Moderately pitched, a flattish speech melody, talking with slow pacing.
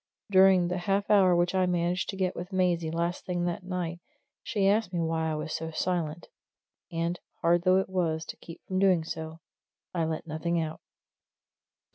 No: medium, 175 Hz; narrow, 2.1 semitones; average, 185 wpm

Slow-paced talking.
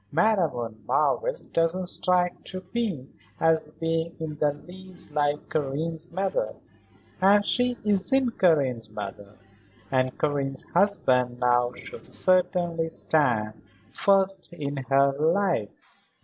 Yes: slow, 110 wpm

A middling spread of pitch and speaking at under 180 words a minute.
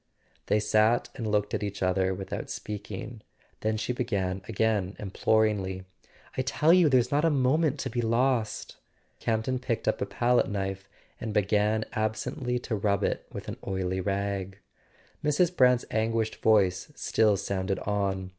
Yes: average, 3.9 semitones; average, 160 wpm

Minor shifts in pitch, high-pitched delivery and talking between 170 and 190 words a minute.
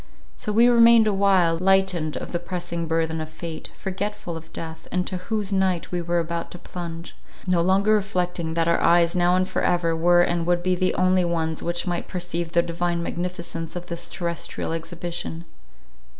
No: narrow, 1.6 semitones; medium, 175 Hz; average, 180 wpm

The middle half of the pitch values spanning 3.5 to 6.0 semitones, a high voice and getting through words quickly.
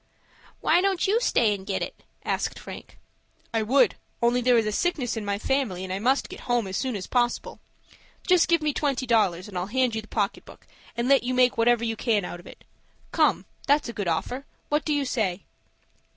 Yes: average, 4.5 semitones; high, 240 Hz; fast, 215 wpm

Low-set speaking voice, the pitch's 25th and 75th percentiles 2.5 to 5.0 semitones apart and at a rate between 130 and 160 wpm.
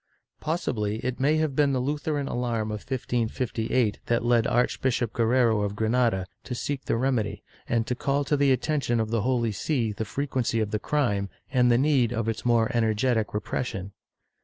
No: low, 120 Hz; average, 3.1 semitones; average, 180 wpm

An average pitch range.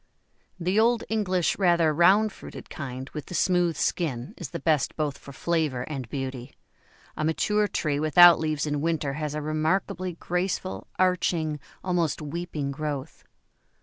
Yes: average, 3.5 semitones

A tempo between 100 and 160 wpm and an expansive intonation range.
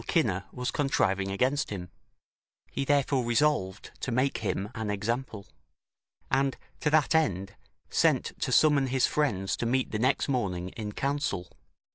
Yes: average, 145 wpm; wide, 5.9 semitones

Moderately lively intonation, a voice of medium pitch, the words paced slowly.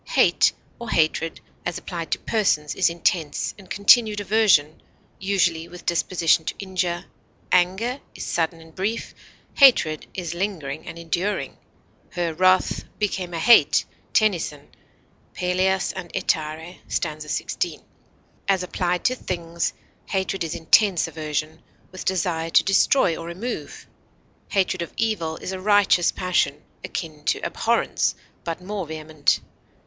Yes: average, 3.0 semitones; medium, 175 Hz; slow, 130 wpm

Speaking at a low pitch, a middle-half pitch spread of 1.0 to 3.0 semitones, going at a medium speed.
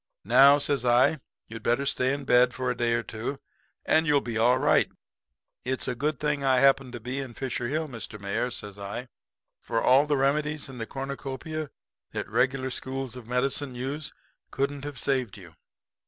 Yes: low, 130 Hz; narrow, 2.5 semitones; average, 190 wpm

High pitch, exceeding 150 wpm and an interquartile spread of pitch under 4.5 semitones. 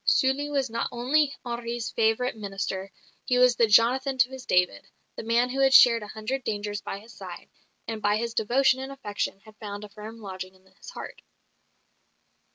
Yes: high, 230 Hz; average, 185 wpm; average, 3.7 semitones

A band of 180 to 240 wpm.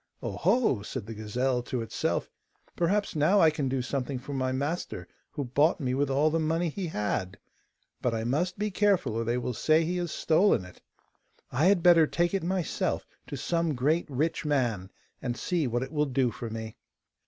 Yes: average, 200 wpm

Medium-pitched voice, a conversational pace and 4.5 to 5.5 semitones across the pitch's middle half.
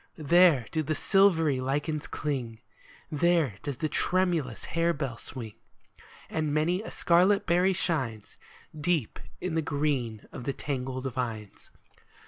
No: medium, 150 Hz; slow, 125 wpm; average, 4.9 semitones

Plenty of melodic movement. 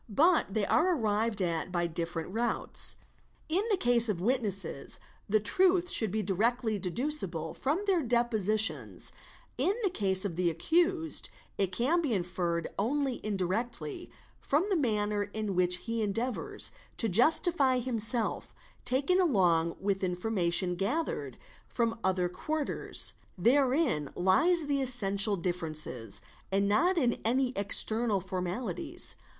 Yes: wide, 6.7 semitones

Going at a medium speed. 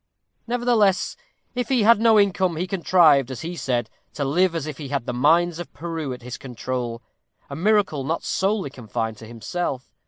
Yes: average, 185 wpm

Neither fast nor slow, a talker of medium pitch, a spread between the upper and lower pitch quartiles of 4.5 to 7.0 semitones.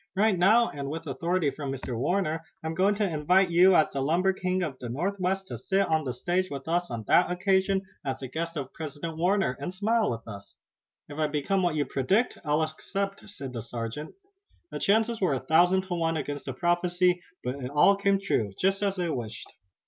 No: fast, 210 wpm; medium, 170 Hz; average, 5.2 semitones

